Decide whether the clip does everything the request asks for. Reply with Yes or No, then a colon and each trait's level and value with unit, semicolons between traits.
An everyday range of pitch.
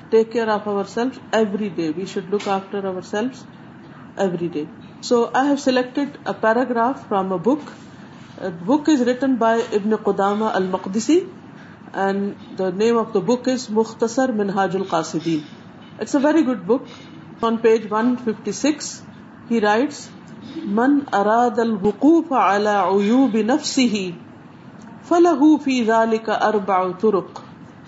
Yes: average, 3.9 semitones